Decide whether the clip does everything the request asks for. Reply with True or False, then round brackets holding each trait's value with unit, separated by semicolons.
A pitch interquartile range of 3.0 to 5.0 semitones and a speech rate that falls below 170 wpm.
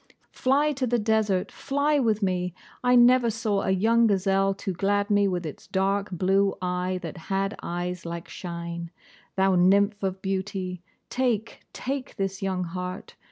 True (3.3 semitones; 160 wpm)